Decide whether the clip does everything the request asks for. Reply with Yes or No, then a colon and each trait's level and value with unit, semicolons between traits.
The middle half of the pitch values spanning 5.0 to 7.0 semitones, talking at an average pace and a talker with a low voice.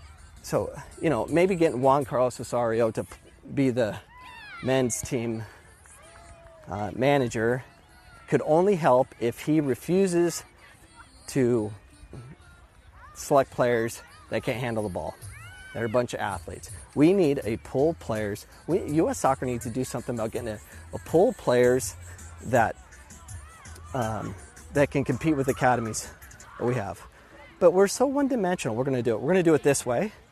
Yes: wide, 5.6 semitones; average, 160 wpm; low, 120 Hz